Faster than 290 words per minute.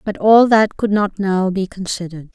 No: fast, 205 wpm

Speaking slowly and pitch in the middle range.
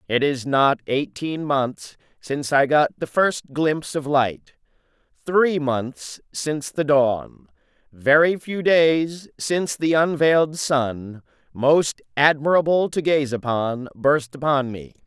Yes: slow, 130 wpm; medium, 145 Hz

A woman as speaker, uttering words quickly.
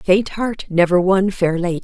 No: female; average, 195 wpm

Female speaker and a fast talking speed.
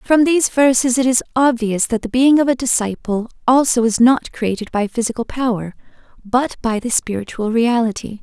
No: female; average, 175 wpm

